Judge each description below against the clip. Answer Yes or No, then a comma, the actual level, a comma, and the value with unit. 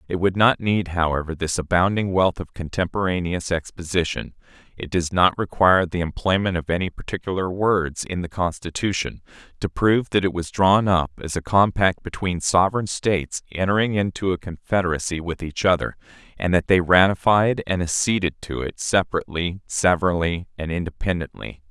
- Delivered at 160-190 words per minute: No, average, 150 wpm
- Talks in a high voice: No, very low, 90 Hz